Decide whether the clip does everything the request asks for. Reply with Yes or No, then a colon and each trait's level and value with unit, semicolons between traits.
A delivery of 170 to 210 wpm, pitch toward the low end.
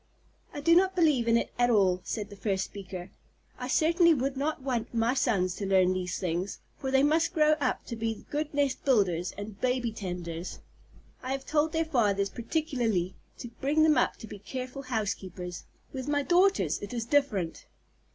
No: average, 185 wpm; high, 240 Hz